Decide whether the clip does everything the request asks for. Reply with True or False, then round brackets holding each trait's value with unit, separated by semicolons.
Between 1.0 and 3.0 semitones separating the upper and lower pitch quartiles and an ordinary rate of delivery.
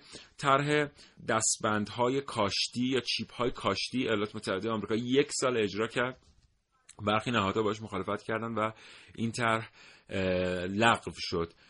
True (2.7 semitones; 125 wpm)